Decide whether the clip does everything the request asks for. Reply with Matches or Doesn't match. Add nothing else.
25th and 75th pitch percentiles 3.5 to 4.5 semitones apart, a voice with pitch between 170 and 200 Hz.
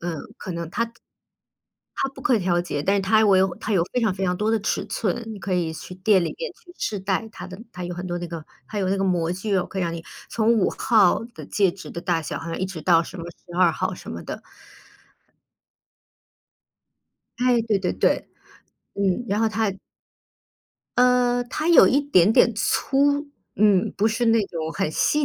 Matches